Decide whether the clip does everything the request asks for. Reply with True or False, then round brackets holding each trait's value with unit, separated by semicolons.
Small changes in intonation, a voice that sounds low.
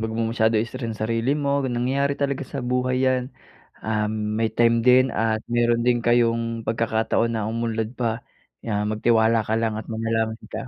True (1.4 semitones; 115 Hz)